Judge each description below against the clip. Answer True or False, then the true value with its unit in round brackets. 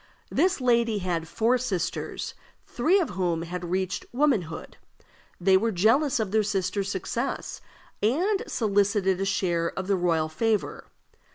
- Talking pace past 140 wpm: False (135 wpm)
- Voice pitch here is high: True (200 Hz)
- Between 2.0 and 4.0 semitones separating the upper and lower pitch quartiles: False (4.5 semitones)